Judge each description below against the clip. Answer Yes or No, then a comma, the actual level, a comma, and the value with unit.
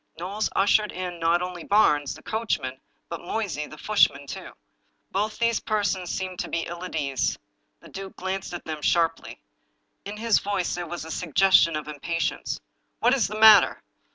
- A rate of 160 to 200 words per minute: Yes, average, 180 wpm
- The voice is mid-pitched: Yes, medium, 180 Hz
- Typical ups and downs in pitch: Yes, average, 4.0 semitones